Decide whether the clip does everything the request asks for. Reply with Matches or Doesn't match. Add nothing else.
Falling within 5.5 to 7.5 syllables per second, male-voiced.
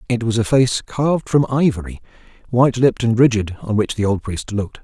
Matches